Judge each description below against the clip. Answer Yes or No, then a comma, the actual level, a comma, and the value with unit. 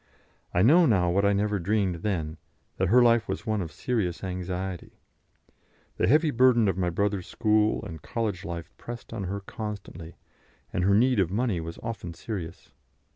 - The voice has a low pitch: Yes, low, 100 Hz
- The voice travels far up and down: No, average, 3.9 semitones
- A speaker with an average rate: Yes, average, 175 wpm